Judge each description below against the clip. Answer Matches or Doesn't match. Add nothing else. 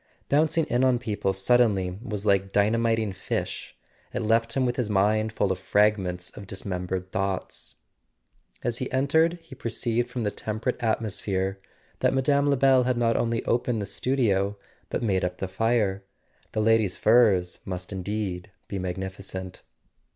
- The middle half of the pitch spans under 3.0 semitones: Doesn't match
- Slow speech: Doesn't match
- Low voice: Matches